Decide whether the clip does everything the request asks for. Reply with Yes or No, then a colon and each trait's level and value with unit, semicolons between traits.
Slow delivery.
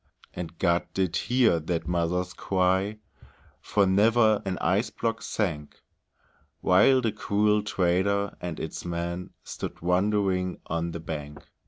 Yes: slow, 130 wpm